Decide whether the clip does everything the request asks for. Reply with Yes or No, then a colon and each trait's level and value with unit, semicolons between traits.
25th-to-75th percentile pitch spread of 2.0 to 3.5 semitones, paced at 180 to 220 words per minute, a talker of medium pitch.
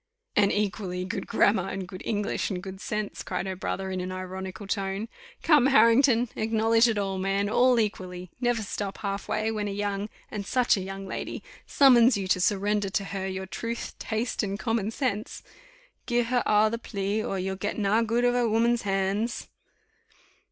No: average, 2.9 semitones; average, 185 wpm; high, 205 Hz